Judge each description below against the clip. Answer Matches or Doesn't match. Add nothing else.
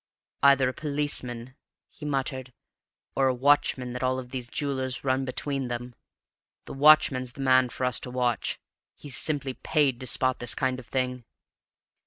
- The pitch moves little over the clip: Matches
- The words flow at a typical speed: Matches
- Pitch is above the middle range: Doesn't match